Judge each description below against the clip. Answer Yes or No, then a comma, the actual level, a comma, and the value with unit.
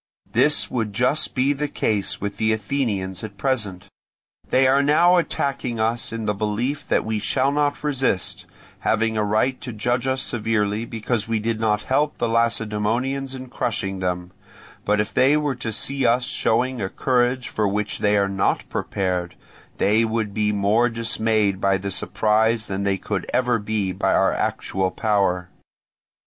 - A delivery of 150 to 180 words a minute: Yes, average, 170 wpm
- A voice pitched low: Yes, low, 110 Hz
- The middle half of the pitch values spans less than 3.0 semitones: No, average, 3.8 semitones